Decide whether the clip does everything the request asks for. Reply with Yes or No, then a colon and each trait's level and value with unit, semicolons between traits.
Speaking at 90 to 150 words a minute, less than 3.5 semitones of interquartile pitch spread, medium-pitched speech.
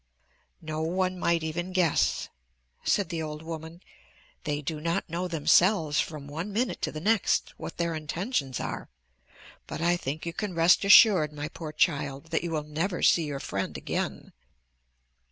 No: average, 165 wpm; average, 2.7 semitones; medium, 160 Hz